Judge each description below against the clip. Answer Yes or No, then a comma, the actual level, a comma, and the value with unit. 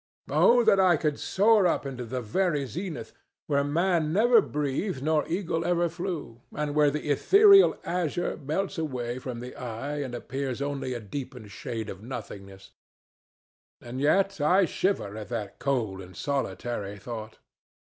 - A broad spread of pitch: Yes, wide, 6.3 semitones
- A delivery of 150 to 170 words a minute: Yes, average, 155 wpm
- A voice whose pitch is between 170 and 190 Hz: No, medium, 145 Hz